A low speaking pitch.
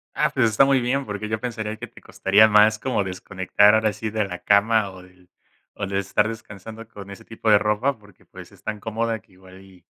Yes: low, 105 Hz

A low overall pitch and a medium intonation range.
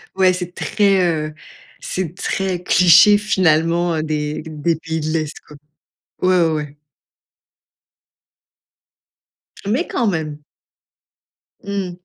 No: medium, 170 Hz; average, 3.3 semitones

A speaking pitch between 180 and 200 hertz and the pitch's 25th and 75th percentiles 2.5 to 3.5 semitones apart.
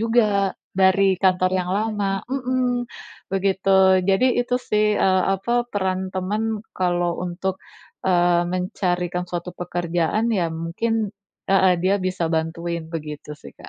Yes: high, 190 Hz; average, 3.0 semitones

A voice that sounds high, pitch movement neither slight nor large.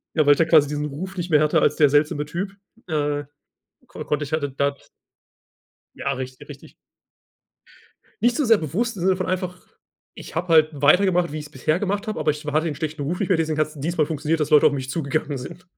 No: medium, 155 Hz; average, 3.4 semitones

